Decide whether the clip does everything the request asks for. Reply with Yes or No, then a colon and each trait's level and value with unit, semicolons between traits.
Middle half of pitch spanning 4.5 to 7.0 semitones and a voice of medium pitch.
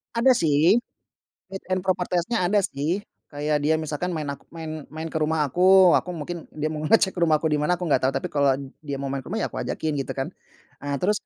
No: average, 3.5 semitones; medium, 160 Hz